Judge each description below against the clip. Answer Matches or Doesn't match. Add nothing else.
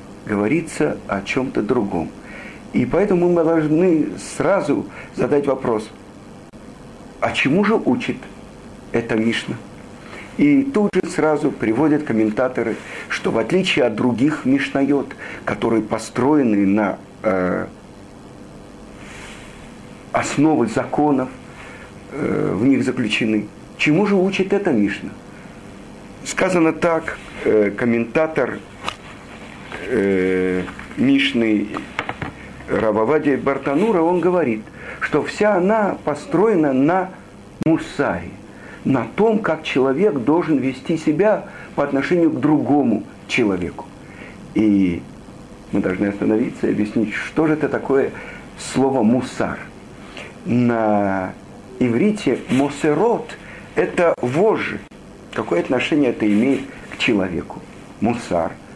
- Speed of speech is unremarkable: Doesn't match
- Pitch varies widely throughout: Matches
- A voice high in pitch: Doesn't match